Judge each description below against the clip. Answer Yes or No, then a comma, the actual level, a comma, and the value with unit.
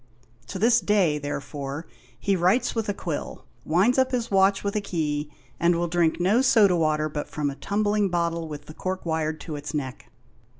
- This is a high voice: No, medium, 170 Hz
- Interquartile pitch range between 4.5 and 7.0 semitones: Yes, average, 4.9 semitones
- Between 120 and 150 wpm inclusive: No, average, 195 wpm